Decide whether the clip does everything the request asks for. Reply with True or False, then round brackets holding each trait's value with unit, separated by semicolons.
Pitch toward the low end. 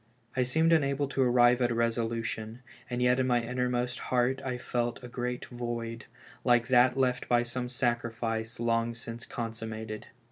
True (120 Hz)